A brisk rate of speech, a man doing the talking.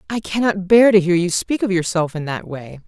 No: fast, 250 wpm; female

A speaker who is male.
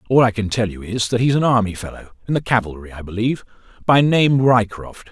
Yes: male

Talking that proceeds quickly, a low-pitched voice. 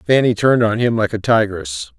Yes: fast, 210 wpm; low, 115 Hz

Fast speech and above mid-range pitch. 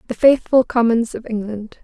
No: average, 165 wpm; high, 230 Hz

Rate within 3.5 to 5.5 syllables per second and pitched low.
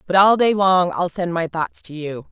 No: 4.7 syllables/s; medium, 180 Hz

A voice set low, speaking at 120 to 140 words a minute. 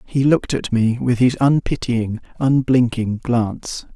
Yes: low, 125 Hz; slow, 135 wpm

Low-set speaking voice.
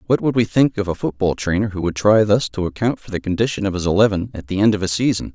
Yes: low, 105 Hz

